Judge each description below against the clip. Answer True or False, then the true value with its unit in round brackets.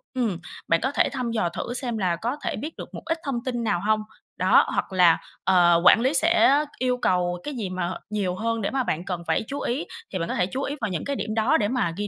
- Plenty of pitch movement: True (6.1 semitones)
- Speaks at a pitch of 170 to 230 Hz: True (220 Hz)